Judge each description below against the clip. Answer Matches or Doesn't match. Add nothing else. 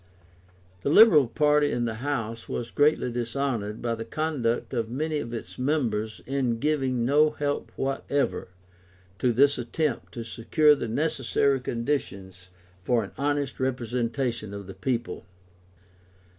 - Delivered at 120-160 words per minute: Matches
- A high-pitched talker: Doesn't match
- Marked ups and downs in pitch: Doesn't match